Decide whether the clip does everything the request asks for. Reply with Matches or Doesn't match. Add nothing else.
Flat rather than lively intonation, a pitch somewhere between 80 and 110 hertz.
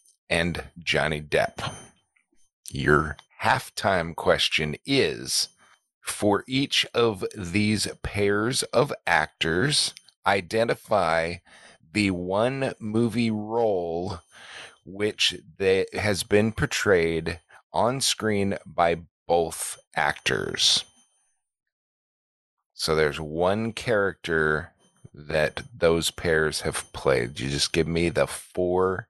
Doesn't match